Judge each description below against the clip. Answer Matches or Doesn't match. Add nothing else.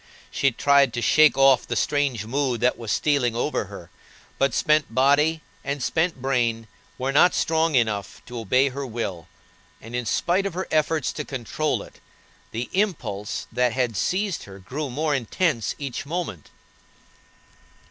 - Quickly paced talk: Doesn't match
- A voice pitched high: Doesn't match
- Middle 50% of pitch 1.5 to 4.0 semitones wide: Doesn't match